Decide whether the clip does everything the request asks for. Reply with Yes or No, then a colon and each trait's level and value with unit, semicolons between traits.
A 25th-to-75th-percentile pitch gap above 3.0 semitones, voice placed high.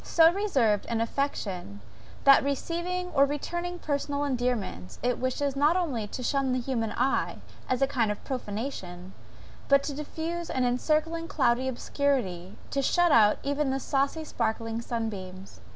Yes: average, 4.4 semitones; very high, 265 Hz